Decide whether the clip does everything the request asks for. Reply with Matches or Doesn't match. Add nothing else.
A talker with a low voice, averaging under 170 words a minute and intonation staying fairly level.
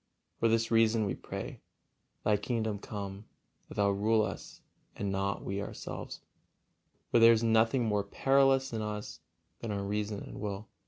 Matches